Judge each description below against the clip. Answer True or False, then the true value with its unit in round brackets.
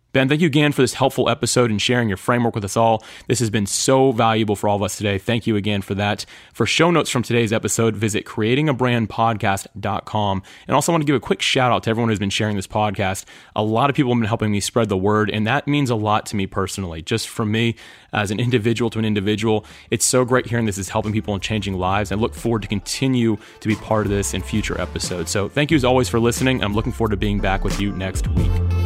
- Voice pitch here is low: True (110 Hz)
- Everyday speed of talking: False (260 wpm)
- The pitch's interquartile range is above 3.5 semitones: False (2.9 semitones)